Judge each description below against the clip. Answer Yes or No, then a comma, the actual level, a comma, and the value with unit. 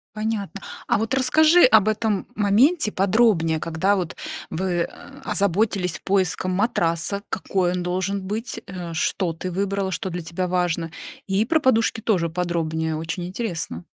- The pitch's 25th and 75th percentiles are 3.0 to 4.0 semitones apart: Yes, average, 3.6 semitones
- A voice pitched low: No, high, 190 Hz